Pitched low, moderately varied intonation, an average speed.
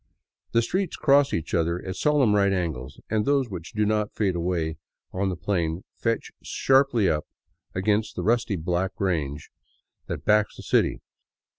Yes: low, 100 Hz; average, 4.9 semitones; average, 160 wpm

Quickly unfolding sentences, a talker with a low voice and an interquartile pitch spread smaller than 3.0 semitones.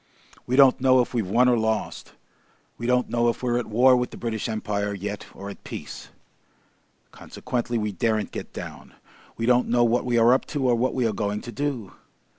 Yes: fast, 210 wpm; low, 120 Hz; narrow, 2.5 semitones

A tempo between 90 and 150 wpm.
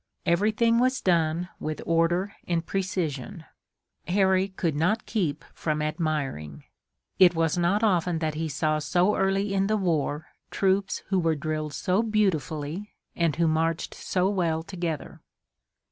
Yes: average, 140 wpm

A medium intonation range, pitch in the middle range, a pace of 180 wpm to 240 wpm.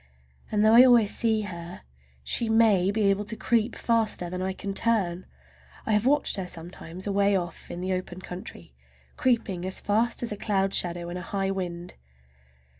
No: average, 3.6 semitones; high, 195 Hz; average, 185 wpm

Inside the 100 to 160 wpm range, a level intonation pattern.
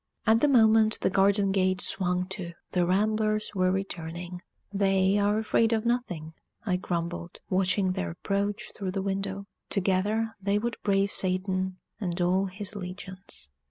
Yes: average, 150 wpm; narrow, 2.1 semitones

